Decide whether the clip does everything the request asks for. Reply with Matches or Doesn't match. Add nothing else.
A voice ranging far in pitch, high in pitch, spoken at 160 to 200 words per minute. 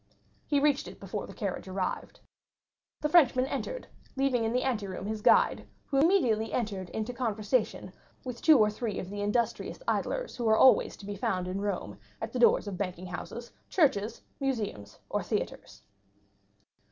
Doesn't match